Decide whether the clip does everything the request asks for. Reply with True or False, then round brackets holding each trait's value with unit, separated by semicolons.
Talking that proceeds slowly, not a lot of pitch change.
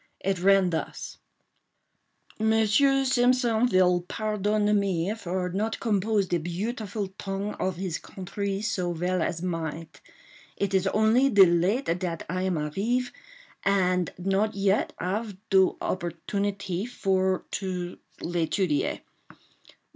False (115 wpm; 3.0 semitones)